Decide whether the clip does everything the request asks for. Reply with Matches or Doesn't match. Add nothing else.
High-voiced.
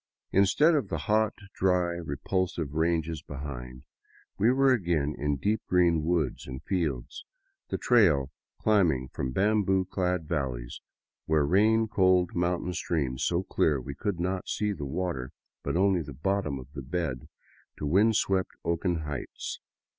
Doesn't match